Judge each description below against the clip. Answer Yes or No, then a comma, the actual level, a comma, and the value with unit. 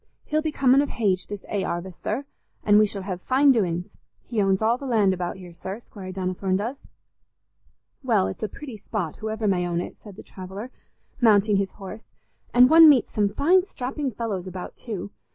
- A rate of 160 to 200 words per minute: Yes, average, 195 wpm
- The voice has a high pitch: Yes, high, 210 Hz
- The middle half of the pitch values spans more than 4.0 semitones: Yes, average, 4.7 semitones